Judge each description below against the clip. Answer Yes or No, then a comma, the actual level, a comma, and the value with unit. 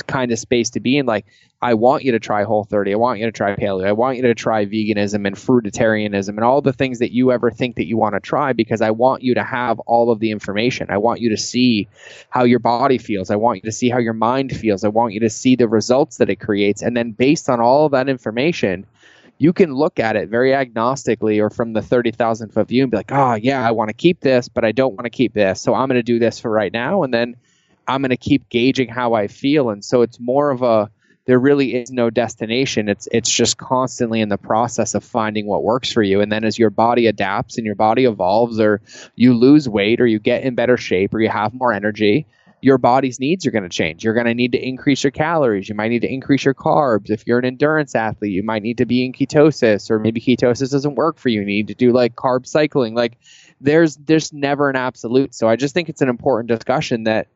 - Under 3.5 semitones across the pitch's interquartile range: Yes, average, 3.0 semitones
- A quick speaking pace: Yes, fast, 260 wpm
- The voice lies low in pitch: Yes, low, 120 Hz